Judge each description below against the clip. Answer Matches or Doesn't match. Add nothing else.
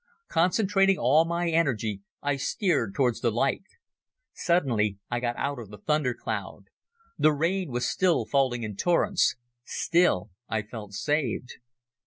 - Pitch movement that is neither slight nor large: Doesn't match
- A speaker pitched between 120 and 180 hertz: Matches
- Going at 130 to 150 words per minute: Matches